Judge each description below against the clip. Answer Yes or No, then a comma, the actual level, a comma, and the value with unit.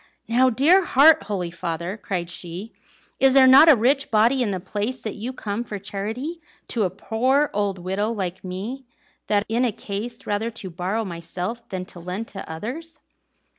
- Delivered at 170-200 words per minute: Yes, average, 185 wpm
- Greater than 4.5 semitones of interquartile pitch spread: Yes, average, 5.2 semitones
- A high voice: Yes, high, 215 Hz